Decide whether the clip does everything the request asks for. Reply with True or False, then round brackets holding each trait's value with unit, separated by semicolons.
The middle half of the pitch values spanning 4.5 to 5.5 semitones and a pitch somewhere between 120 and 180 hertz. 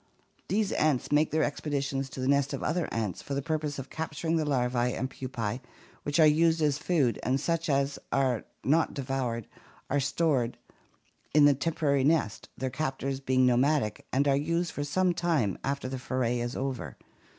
False (3.2 semitones; 140 Hz)